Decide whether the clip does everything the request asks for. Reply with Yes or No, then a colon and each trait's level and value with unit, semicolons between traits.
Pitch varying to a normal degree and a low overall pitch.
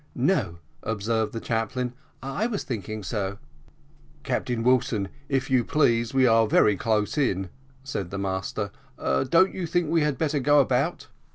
Yes: average, 5.0 semitones; low, 120 Hz